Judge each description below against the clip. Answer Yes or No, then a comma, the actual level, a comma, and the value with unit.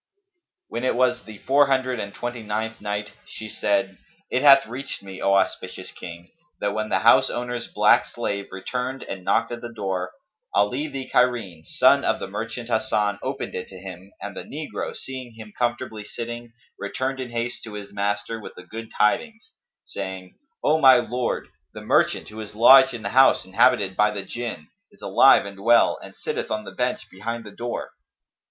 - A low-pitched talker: Yes, low, 110 Hz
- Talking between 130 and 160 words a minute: No, average, 185 wpm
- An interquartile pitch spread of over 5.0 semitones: No, average, 3.6 semitones